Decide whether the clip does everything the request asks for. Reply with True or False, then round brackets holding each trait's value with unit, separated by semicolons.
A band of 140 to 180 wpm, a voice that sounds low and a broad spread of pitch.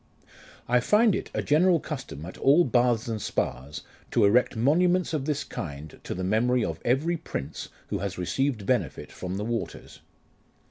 True (170 wpm; 120 Hz; 7.1 semitones)